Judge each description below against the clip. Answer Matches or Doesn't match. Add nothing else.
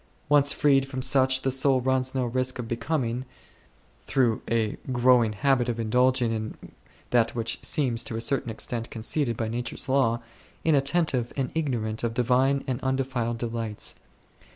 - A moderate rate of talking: Matches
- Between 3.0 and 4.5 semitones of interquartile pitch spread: Doesn't match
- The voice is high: Doesn't match